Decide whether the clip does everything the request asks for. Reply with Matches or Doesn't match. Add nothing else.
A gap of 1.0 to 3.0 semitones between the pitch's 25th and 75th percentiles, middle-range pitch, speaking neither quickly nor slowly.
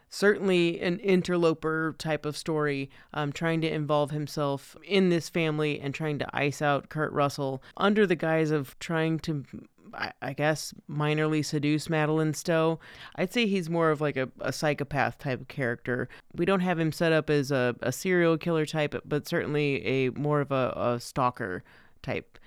Matches